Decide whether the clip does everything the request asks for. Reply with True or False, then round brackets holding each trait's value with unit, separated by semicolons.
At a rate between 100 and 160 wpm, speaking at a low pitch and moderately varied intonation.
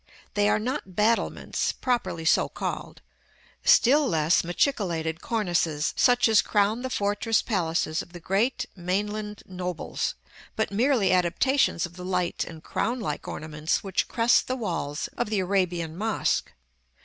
False (140 wpm; 195 Hz; 4.7 semitones)